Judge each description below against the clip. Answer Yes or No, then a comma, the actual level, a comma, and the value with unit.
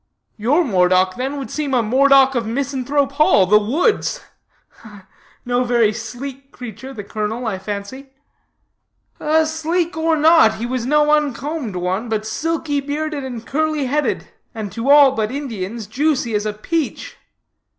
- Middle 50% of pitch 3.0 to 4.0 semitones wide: No, average, 5.1 semitones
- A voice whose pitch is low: No, very high, 260 Hz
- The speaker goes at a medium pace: Yes, average, 145 wpm